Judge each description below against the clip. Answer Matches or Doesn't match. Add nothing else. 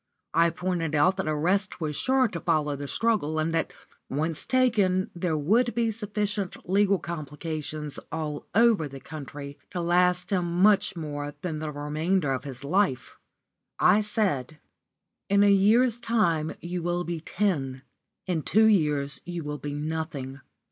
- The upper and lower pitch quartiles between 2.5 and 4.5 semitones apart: Doesn't match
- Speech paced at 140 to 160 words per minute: Matches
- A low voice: Doesn't match